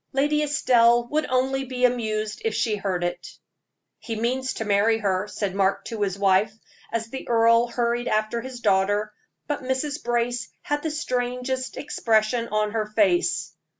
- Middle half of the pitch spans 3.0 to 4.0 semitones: Yes, average, 3.3 semitones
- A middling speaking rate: Yes, average, 160 wpm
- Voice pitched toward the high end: Yes, high, 235 Hz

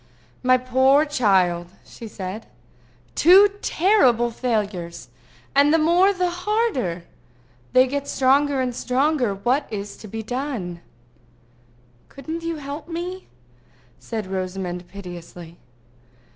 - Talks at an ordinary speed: No, slow, 110 wpm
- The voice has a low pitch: No, very high, 255 Hz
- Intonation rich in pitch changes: Yes, wide, 7.7 semitones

